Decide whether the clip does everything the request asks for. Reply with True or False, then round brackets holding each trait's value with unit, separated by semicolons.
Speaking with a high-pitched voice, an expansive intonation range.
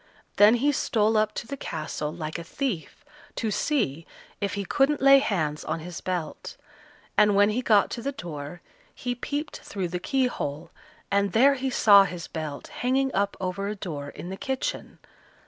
True (200 Hz; 6.8 semitones)